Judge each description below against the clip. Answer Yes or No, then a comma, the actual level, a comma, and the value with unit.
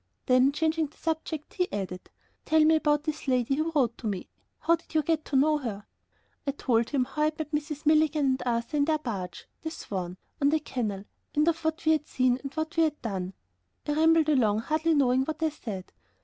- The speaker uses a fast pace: Yes, fast, 220 wpm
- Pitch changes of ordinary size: Yes, average, 4.3 semitones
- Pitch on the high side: Yes, very high, 295 Hz